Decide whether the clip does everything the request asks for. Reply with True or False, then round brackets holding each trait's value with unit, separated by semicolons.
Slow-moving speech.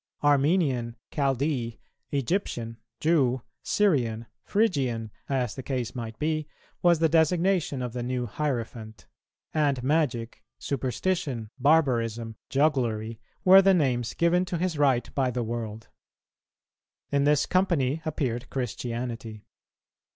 True (115 wpm)